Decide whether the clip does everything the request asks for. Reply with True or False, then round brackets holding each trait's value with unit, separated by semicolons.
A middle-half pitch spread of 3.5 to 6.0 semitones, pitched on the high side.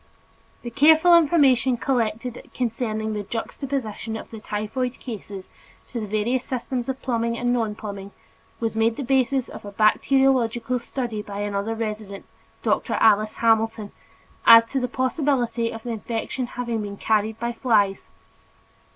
False (2.8 semitones; 230 Hz)